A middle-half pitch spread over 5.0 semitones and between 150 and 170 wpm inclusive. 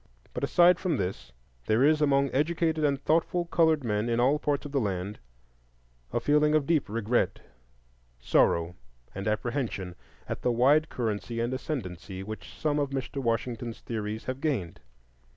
Yes: wide, 5.6 semitones; average, 155 wpm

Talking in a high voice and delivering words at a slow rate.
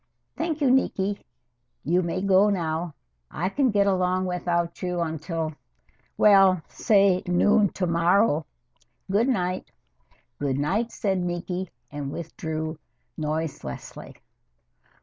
No: medium, 180 Hz; slow, 110 wpm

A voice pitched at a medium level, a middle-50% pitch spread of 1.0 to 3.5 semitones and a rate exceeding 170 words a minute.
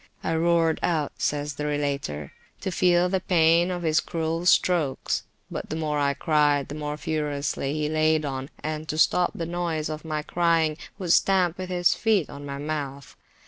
Yes: medium, 155 Hz; average, 2.7 semitones; average, 185 wpm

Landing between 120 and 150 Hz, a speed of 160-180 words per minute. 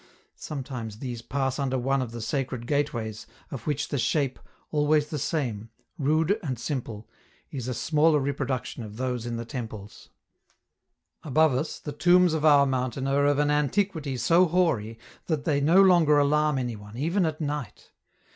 Yes: medium, 140 Hz; average, 165 wpm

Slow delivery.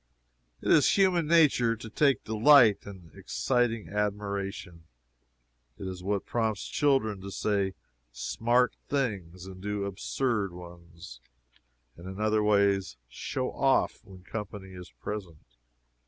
Yes: slow, 125 wpm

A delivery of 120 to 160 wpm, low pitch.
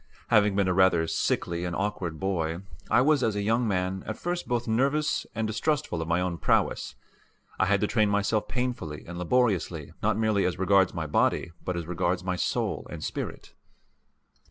No: average, 185 wpm; very low, 95 Hz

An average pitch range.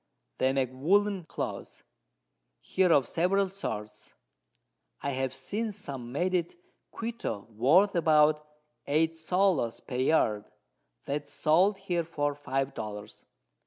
No: wide, 5.7 semitones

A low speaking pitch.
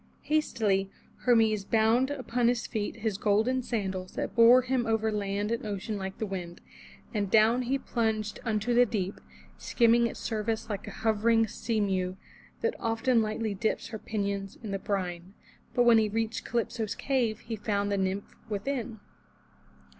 No: high, 220 Hz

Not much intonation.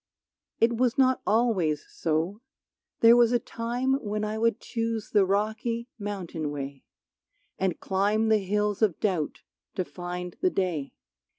No: average, 4.3 semitones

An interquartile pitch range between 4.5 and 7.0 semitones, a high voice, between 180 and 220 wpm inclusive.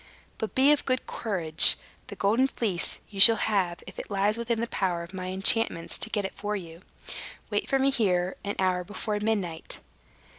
No: average, 3.8 semitones; high, 205 Hz; average, 190 wpm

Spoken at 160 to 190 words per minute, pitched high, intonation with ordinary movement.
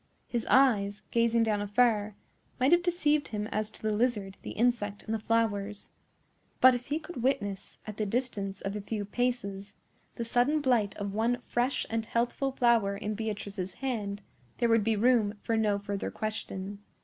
Yes: average, 175 wpm; high, 220 Hz; average, 3.2 semitones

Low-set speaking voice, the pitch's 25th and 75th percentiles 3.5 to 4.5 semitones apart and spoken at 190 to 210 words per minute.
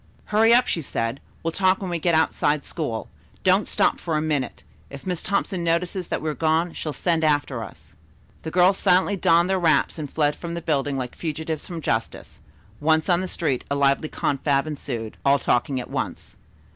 No: medium, 160 Hz; average, 3.9 semitones; average, 195 wpm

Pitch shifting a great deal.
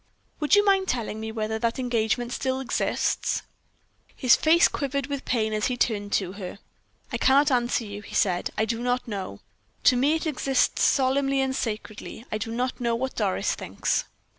No: average, 3.6 semitones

